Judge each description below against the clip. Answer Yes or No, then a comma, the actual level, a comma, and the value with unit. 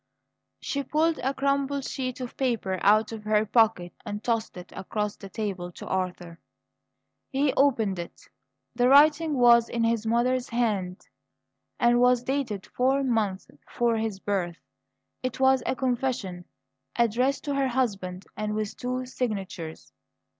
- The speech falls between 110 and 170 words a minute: Yes, average, 145 wpm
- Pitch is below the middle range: No, high, 235 Hz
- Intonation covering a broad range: No, average, 4.4 semitones